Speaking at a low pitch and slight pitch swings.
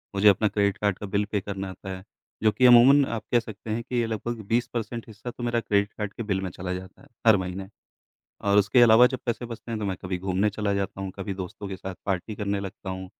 No: low, 105 Hz; average, 3.1 semitones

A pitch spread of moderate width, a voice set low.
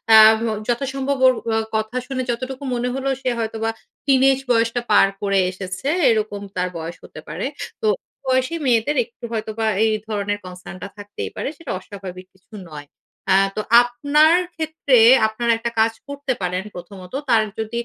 No: average, 4.5 semitones; high, 225 Hz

